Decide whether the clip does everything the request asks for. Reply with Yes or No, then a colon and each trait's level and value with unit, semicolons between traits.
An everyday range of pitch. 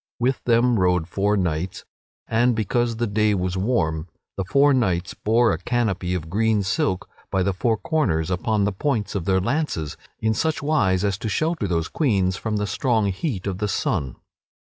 Yes: average, 4.4 semitones